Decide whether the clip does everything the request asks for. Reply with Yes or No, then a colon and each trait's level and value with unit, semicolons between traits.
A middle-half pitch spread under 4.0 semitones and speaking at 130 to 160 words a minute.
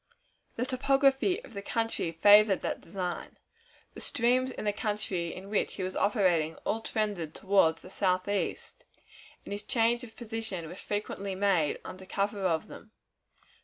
Yes: average, 3.5 semitones; average, 155 wpm